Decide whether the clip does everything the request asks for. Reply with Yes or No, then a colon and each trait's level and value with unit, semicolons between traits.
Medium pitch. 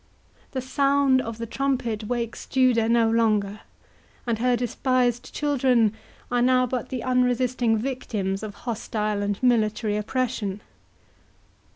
No: high, 235 Hz